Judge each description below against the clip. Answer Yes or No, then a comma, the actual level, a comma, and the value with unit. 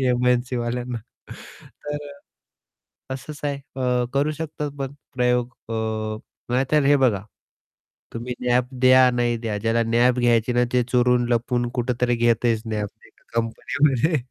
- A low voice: Yes, low, 125 Hz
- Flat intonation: Yes, narrow, 1.7 semitones